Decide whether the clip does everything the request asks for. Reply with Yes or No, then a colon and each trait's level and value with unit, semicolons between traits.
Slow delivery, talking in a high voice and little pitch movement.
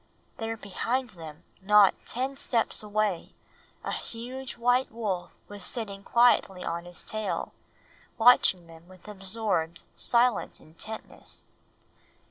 No: slow, 110 wpm; high, 210 Hz; average, 4.3 semitones